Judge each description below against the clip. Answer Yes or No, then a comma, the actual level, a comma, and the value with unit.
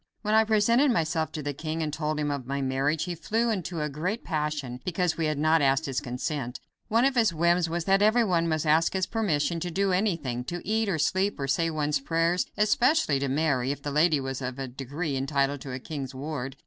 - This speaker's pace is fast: Yes, fast, 230 wpm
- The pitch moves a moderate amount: Yes, average, 4.5 semitones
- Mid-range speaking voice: Yes, medium, 155 Hz